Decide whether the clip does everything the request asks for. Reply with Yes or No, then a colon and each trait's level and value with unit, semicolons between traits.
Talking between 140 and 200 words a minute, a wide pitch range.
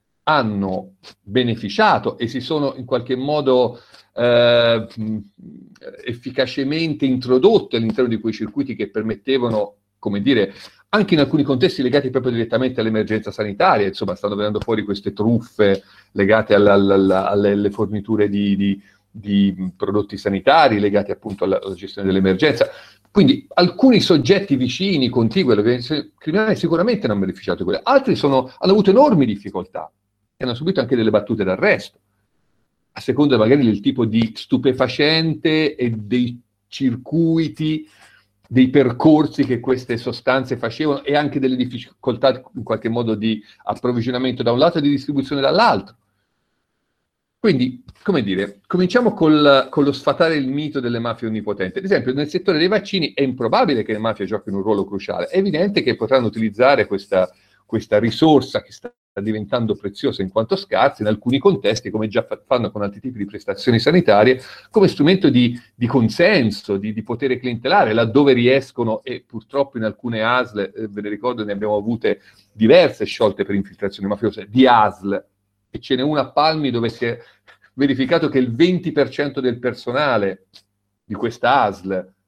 No: average, 150 wpm; average, 4.9 semitones